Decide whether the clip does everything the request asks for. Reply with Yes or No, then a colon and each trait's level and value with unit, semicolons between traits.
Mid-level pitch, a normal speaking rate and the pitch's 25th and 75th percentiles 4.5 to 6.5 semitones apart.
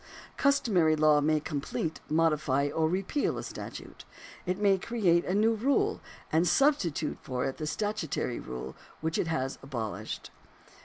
Yes: medium, 160 Hz; average, 145 wpm; wide, 5.6 semitones